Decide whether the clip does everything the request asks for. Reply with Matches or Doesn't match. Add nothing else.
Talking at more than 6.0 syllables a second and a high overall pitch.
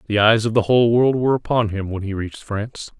Doesn't match